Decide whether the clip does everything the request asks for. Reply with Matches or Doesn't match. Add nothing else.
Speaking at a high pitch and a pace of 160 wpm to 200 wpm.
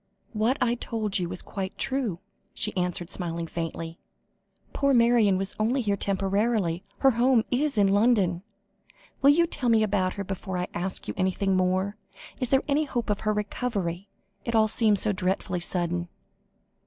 Matches